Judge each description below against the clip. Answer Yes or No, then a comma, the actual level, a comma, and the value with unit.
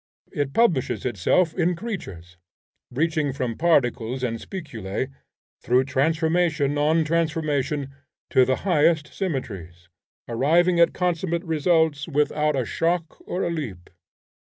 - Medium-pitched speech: Yes, medium, 150 Hz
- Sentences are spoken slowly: Yes, slow, 115 wpm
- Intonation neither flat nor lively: Yes, average, 4.6 semitones